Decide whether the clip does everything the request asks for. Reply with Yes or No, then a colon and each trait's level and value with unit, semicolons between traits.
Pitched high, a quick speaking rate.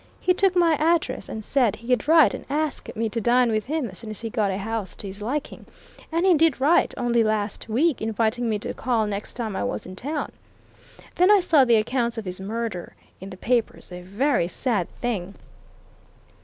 Yes: high, 230 Hz; fast, 210 wpm